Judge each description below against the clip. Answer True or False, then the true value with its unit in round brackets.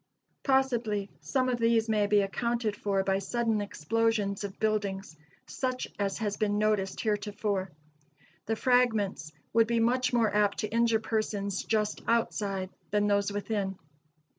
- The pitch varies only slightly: True (2.3 semitones)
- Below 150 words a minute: True (140 wpm)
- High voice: True (210 Hz)